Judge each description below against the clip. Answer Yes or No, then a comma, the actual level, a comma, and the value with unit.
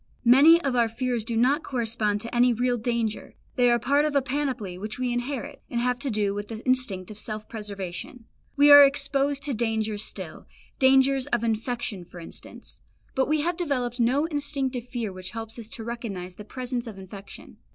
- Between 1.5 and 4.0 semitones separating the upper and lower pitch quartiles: Yes, average, 3.6 semitones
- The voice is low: No, high, 240 Hz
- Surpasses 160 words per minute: Yes, average, 195 wpm